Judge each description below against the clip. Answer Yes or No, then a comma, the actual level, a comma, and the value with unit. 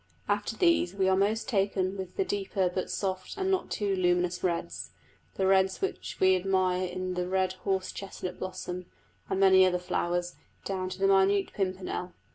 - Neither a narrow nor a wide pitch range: No, narrow, 1.2 semitones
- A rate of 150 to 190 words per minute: Yes, average, 175 wpm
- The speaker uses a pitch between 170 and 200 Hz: Yes, high, 190 Hz